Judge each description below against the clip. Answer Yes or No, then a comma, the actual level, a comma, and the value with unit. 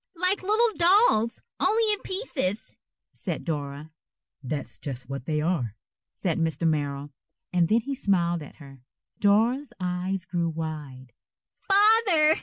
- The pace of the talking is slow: Yes, slow, 130 wpm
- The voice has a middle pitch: Yes, medium, 180 Hz